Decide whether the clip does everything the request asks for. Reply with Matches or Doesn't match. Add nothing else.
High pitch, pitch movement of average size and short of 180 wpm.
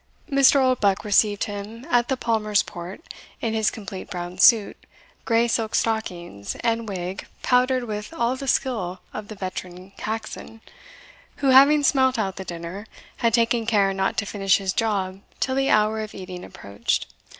Matches